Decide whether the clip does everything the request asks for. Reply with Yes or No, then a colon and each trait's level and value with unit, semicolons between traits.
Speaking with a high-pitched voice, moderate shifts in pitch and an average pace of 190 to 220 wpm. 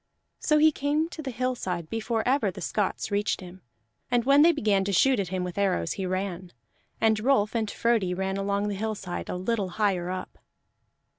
Yes: high, 205 Hz; average, 4.4 semitones; average, 195 wpm